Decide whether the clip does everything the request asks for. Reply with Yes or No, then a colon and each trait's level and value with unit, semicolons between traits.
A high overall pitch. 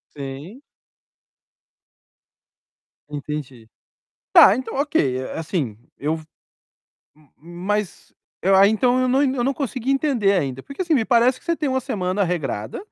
Yes: high, 205 Hz